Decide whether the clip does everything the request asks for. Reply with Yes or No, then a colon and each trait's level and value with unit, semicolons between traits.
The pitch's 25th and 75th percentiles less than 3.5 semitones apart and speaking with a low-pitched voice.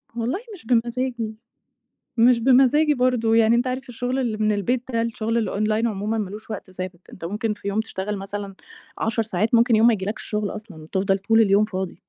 No: average, 2.7 semitones; high, 220 Hz